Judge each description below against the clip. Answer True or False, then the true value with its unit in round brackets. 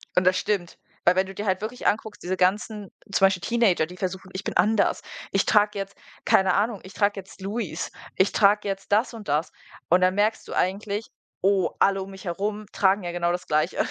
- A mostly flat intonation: True (2.1 semitones)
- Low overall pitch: False (195 Hz)